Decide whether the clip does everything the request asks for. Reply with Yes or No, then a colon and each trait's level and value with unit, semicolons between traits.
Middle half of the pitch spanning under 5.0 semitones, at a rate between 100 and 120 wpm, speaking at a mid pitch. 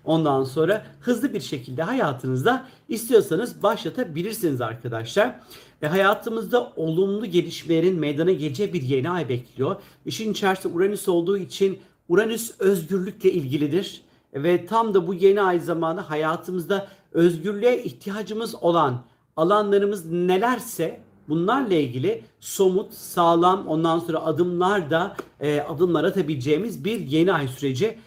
Yes: average, 4.1 semitones; average, 115 wpm; medium, 180 Hz